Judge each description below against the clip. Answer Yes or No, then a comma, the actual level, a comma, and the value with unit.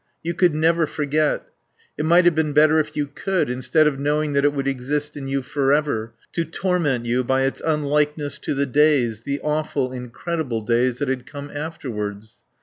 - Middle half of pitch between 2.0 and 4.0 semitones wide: Yes, average, 3.1 semitones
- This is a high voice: No, medium, 145 Hz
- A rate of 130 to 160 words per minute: No, average, 185 wpm